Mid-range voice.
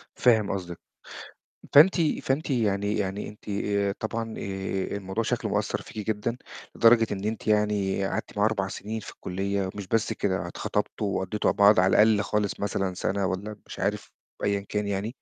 No: low, 100 Hz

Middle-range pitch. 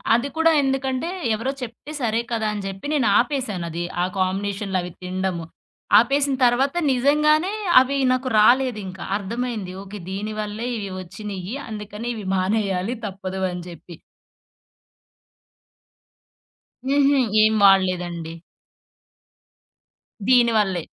No: high, 210 Hz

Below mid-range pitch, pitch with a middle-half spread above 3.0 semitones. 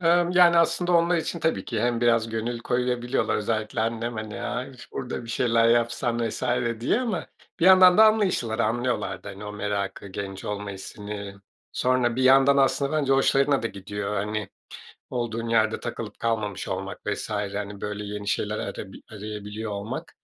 Yes: low, 115 Hz; average, 4.2 semitones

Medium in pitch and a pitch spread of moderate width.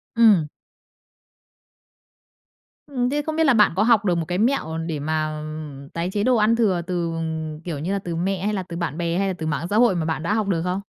Yes: medium, 180 Hz; average, 4.7 semitones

